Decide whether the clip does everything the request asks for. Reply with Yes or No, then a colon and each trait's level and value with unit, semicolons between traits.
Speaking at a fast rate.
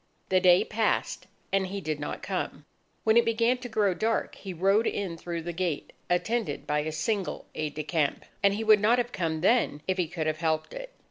Yes: fast, 215 wpm